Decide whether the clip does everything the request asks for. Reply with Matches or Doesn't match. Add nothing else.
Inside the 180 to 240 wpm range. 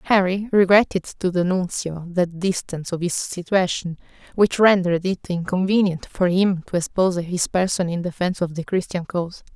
Doesn't match